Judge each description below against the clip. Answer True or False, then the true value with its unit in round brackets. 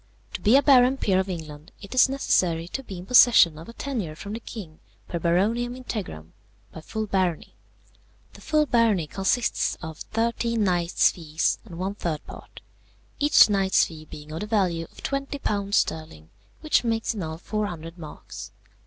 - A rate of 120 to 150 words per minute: False (170 wpm)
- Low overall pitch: False (195 Hz)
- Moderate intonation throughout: False (5.9 semitones)